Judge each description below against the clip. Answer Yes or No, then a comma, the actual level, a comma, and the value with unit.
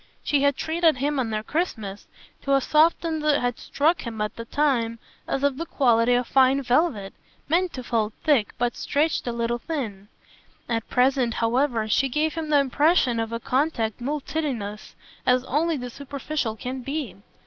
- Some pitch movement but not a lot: Yes, average, 4.4 semitones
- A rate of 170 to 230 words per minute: Yes, average, 175 wpm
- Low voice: No, very high, 260 Hz